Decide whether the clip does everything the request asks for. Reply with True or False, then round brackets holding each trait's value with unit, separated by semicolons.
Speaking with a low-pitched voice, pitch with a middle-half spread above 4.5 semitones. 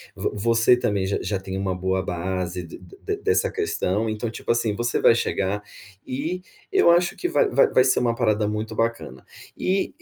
True (110 Hz; 5.1 semitones)